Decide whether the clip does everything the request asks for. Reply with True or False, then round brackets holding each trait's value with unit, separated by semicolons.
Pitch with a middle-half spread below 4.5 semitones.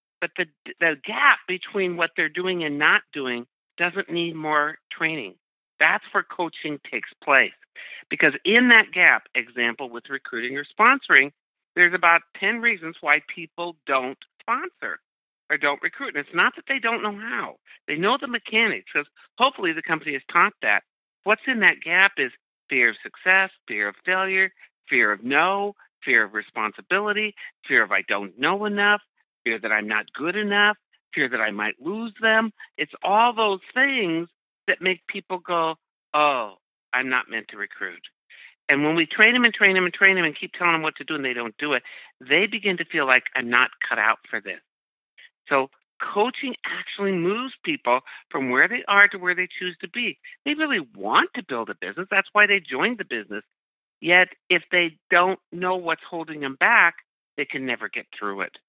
False (4.9 semitones)